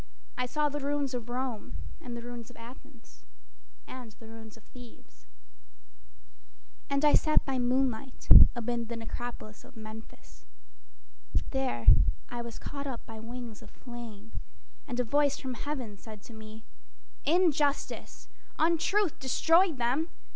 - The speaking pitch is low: No, high, 245 Hz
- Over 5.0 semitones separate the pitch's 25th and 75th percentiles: No, average, 3.8 semitones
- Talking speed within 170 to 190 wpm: No, average, 140 wpm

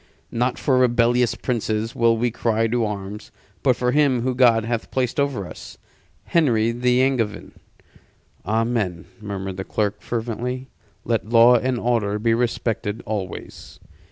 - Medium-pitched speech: No, low, 115 Hz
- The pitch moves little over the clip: Yes, narrow, 2.3 semitones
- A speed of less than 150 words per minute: Yes, average, 140 wpm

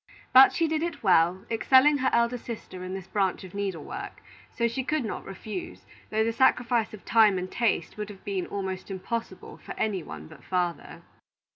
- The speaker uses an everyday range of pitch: Yes, average, 4.0 semitones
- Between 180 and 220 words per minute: Yes, average, 190 wpm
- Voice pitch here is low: No, high, 210 Hz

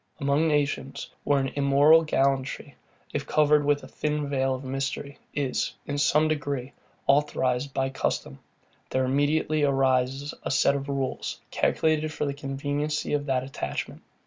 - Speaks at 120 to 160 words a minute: Yes, average, 145 wpm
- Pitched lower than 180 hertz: Yes, medium, 140 Hz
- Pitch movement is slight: Yes, narrow, 1.5 semitones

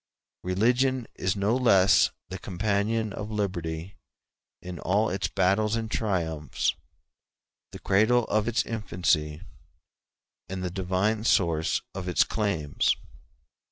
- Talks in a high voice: No, low, 100 Hz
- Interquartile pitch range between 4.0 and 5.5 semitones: No, average, 3.4 semitones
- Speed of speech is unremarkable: No, slow, 120 wpm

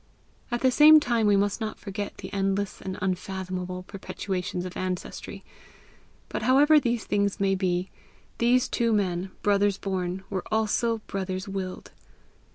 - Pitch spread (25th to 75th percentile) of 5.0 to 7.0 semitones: No, average, 3.0 semitones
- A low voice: No, high, 195 Hz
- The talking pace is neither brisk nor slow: Yes, average, 145 wpm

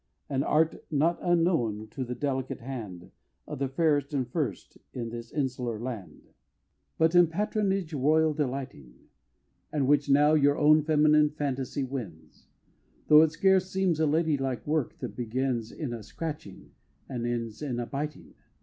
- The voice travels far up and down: No, average, 4.1 semitones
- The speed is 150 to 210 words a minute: Yes, average, 155 wpm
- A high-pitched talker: No, medium, 140 Hz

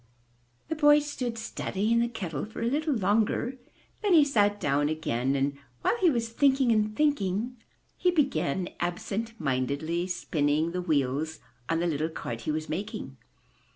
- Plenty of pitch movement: Yes, wide, 7.7 semitones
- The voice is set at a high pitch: Yes, high, 200 Hz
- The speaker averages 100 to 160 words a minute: Yes, average, 155 wpm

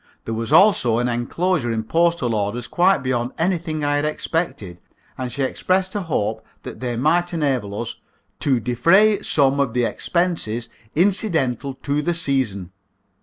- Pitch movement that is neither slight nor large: No, wide, 6.3 semitones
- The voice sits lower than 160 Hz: Yes, medium, 140 Hz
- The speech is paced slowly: No, average, 155 wpm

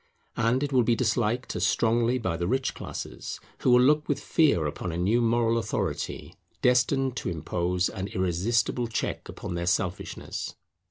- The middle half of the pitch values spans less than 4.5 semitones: No, wide, 5.5 semitones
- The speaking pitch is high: No, low, 115 Hz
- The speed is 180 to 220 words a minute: No, average, 165 wpm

